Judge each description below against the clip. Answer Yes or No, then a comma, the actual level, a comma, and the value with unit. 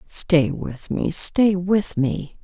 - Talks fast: No, average, 150 wpm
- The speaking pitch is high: No, medium, 175 Hz